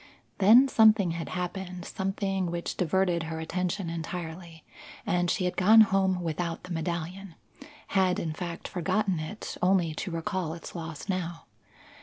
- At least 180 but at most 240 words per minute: No, average, 145 wpm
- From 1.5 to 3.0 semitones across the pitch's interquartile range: Yes, narrow, 2.4 semitones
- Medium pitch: Yes, medium, 180 Hz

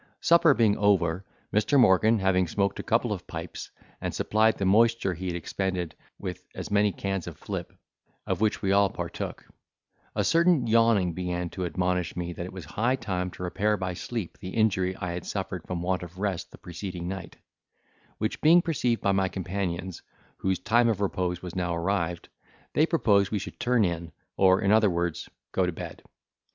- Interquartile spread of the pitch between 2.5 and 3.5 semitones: Yes, average, 3.1 semitones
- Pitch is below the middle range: Yes, very low, 95 Hz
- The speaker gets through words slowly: No, average, 190 wpm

